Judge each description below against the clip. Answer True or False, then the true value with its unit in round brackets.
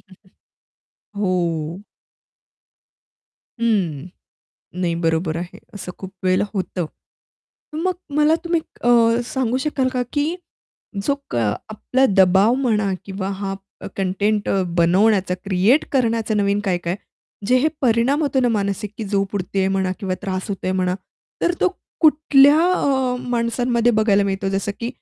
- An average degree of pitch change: True (5.0 semitones)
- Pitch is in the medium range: False (205 Hz)